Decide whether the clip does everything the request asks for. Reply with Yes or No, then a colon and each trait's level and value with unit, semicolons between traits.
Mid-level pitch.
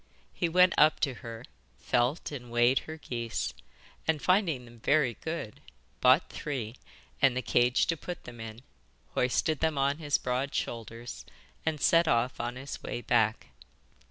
No: low, 125 Hz